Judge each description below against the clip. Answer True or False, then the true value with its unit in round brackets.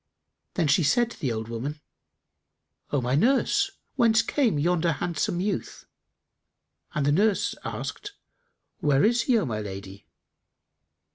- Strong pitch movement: True (8.8 semitones)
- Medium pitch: True (160 Hz)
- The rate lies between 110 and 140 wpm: True (135 wpm)